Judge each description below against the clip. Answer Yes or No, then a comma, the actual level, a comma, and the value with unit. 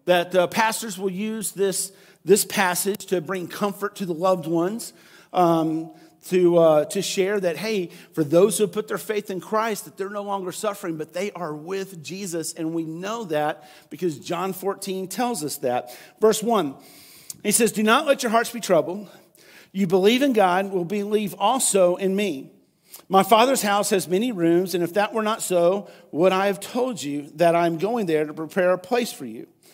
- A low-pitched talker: No, high, 190 Hz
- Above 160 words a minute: Yes, average, 200 wpm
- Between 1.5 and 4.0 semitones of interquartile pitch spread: Yes, average, 3.2 semitones